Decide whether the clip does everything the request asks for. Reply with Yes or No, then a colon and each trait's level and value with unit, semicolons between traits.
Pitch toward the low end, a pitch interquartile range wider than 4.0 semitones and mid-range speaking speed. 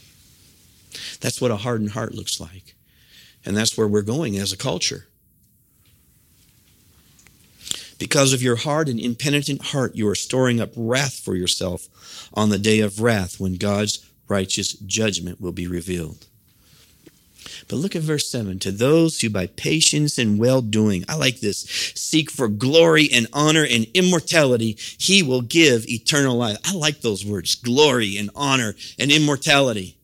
Yes: low, 115 Hz; average, 5.3 semitones; average, 155 wpm